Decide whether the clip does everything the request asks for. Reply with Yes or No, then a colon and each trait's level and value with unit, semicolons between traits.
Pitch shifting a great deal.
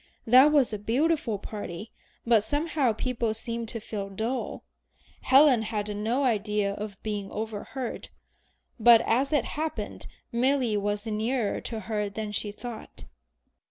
No: average, 3.3 semitones